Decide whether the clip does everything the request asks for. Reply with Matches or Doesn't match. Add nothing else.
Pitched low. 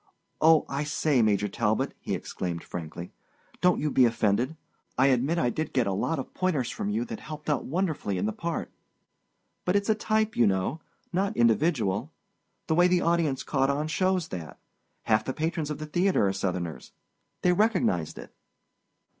Doesn't match